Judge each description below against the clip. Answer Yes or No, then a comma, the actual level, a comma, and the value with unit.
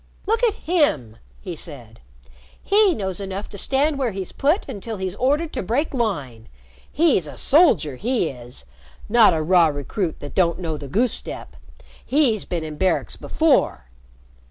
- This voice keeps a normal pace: Yes, average, 160 wpm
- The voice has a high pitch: Yes, high, 195 Hz